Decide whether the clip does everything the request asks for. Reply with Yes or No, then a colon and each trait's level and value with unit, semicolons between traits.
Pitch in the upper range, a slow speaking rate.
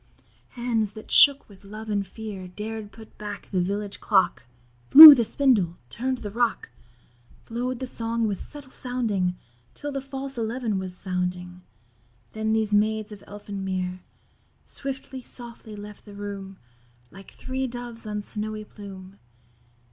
No: high, 215 Hz; average, 145 wpm